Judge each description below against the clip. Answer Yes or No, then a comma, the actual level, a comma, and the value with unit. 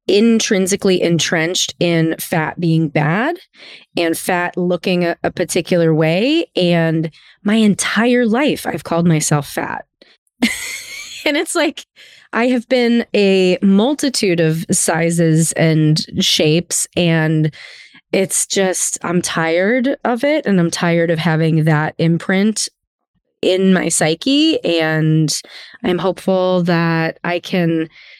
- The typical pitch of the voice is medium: Yes, medium, 175 Hz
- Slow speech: Yes, slow, 120 wpm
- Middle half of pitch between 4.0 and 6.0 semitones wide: No, average, 3.6 semitones